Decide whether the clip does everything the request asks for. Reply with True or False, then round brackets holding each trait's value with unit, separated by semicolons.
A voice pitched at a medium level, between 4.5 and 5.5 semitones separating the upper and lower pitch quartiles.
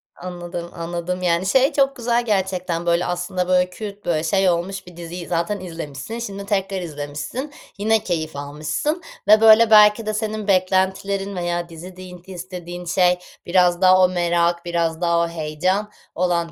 False (180 Hz; 2.6 semitones)